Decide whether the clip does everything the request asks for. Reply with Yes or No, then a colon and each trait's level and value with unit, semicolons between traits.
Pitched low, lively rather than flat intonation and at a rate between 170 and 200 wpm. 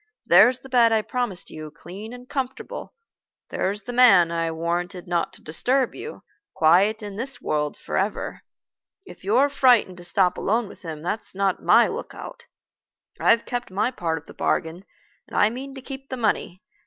No: high, 205 Hz; wide, 6.0 semitones; average, 175 wpm